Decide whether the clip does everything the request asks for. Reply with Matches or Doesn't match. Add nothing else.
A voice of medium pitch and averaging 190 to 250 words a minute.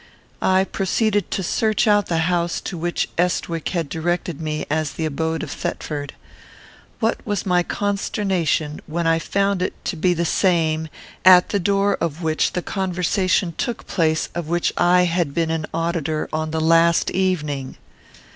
Doesn't match